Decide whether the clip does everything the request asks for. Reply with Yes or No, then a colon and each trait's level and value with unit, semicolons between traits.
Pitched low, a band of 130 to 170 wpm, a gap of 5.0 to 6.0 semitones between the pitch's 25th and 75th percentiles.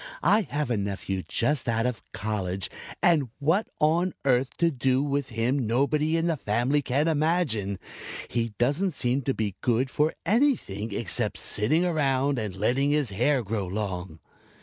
Yes: low, 130 Hz; average, 160 wpm; wide, 5.6 semitones